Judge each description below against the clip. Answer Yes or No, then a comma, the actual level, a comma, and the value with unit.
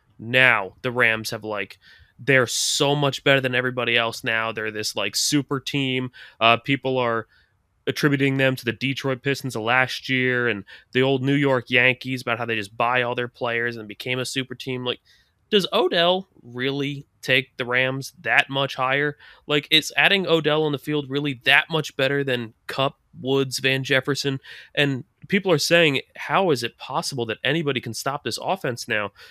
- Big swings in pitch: No, average, 2.7 semitones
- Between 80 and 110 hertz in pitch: No, low, 130 Hz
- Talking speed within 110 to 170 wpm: No, average, 185 wpm